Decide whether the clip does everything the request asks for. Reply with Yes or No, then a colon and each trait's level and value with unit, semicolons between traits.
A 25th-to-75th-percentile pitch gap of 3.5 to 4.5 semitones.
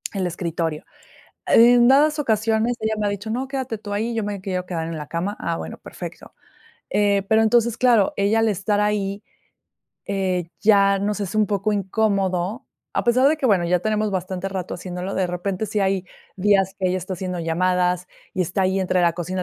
No: average, 3.1 semitones